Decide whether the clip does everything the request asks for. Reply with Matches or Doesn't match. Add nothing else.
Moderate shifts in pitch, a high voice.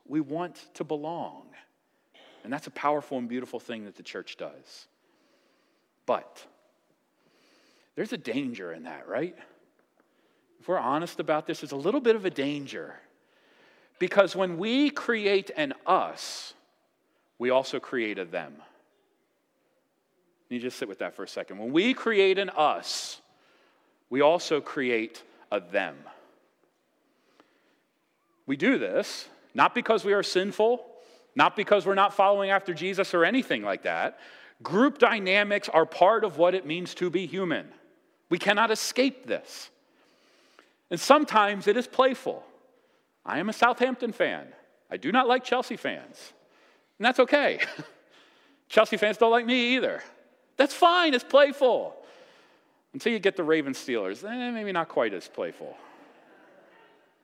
Doesn't match